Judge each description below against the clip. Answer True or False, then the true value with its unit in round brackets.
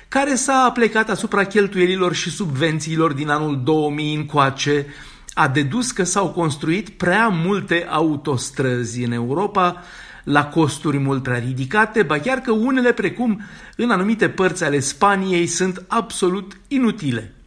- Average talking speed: True (135 wpm)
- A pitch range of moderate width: False (5.7 semitones)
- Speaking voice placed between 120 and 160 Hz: False (175 Hz)